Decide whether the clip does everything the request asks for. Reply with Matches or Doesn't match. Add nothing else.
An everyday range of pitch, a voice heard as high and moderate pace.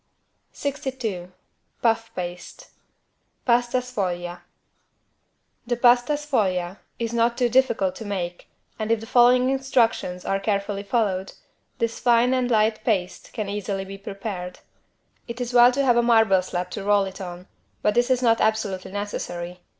Matches